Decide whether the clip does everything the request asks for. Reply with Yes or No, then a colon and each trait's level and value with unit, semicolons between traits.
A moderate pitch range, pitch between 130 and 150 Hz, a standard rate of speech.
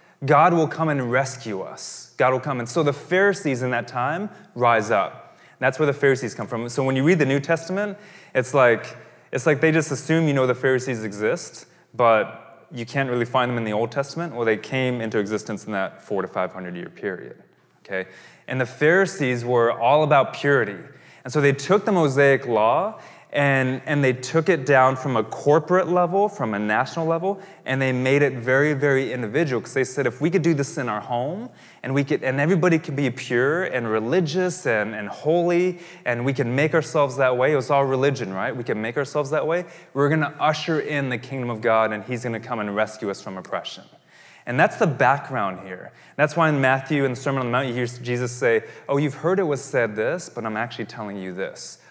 No: average, 4.4 semitones; low, 135 Hz; fast, 225 wpm